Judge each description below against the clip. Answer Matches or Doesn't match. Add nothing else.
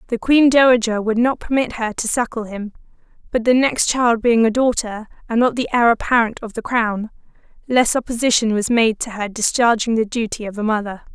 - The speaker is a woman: Matches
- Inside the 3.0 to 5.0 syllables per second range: Doesn't match